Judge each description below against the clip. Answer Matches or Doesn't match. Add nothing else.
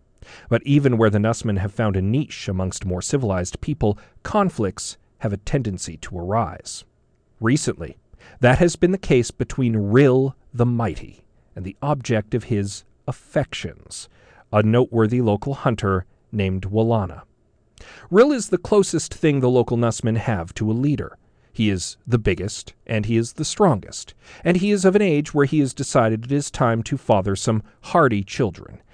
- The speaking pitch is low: Matches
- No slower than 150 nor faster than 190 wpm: Matches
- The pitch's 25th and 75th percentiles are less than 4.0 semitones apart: Doesn't match